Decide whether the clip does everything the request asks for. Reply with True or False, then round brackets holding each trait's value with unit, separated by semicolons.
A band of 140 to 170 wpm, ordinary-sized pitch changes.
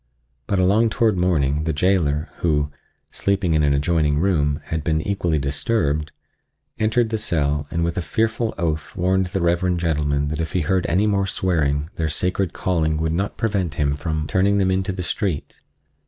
False (180 wpm; 4.1 semitones)